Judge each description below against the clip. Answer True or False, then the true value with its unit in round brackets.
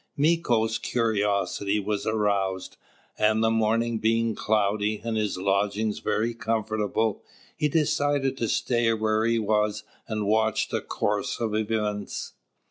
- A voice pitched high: False (110 Hz)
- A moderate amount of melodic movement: False (1.6 semitones)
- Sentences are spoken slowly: True (125 wpm)